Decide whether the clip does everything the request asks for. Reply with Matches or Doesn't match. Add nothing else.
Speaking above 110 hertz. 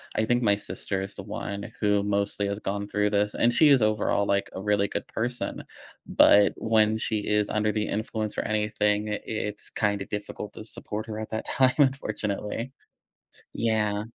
Doesn't match